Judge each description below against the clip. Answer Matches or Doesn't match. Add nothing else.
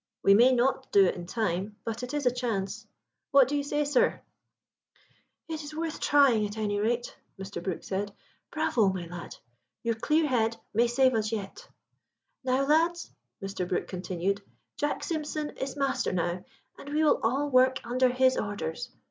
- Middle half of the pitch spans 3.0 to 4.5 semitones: Doesn't match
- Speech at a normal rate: Matches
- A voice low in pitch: Doesn't match